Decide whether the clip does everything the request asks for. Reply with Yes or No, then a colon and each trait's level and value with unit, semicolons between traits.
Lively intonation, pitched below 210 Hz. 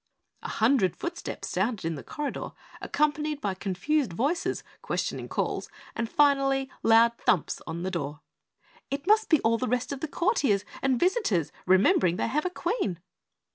No: wide, 7.8 semitones; very high, 250 Hz